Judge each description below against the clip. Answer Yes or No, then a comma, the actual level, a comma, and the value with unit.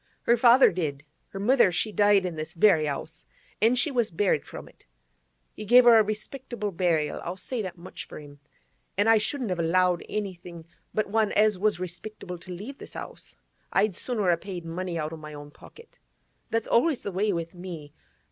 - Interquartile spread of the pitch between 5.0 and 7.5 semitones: No, average, 4.3 semitones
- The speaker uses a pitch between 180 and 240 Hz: Yes, high, 190 Hz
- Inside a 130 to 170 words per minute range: No, average, 195 wpm